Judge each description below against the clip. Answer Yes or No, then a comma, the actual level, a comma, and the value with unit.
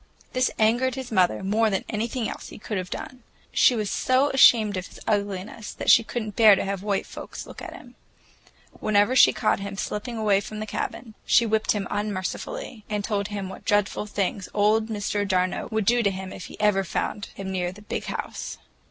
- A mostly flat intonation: Yes, narrow, 2.2 semitones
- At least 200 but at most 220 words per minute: Yes, fast, 205 wpm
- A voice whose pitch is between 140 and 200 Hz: No, high, 210 Hz